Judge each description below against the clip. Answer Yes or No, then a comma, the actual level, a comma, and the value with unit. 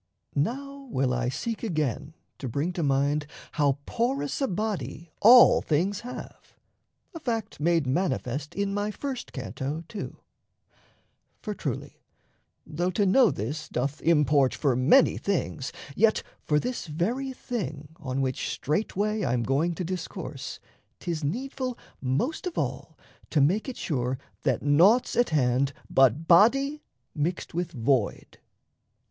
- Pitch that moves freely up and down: Yes, wide, 7.7 semitones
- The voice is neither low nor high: Yes, medium, 165 Hz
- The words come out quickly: No, slow, 135 wpm